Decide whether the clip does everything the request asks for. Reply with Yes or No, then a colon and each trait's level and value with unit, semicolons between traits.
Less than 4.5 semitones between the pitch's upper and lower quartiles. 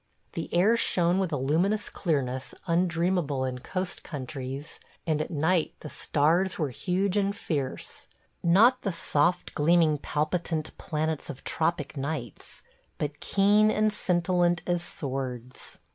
Yes: average, 4.1 semitones